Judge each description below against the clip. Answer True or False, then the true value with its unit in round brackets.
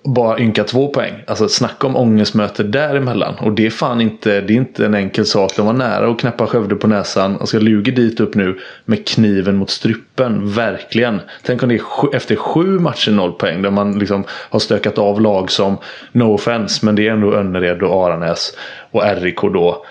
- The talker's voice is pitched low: True (110 Hz)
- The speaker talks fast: True (210 wpm)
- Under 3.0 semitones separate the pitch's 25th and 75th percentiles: True (2.5 semitones)